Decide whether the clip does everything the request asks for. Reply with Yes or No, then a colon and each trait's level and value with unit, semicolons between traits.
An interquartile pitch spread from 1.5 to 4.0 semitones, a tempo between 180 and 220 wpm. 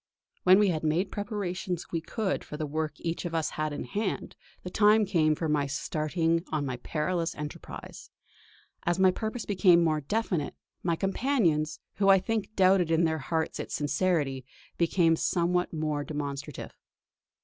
No: average, 3.7 semitones; average, 165 wpm